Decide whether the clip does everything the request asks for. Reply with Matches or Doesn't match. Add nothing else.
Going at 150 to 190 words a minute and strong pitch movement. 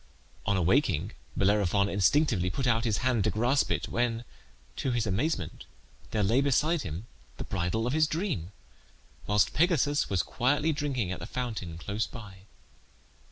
Matches